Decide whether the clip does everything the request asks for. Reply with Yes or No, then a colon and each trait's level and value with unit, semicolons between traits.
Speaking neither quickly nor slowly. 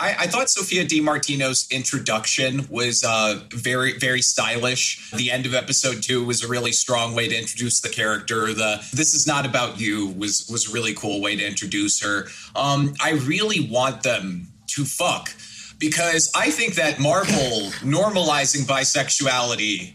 Yes: average, 160 wpm